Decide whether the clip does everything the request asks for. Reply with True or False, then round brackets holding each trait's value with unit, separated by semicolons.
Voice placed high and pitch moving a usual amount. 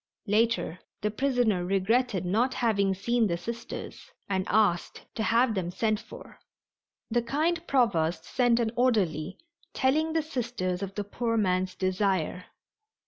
True (215 Hz; 4.5 semitones)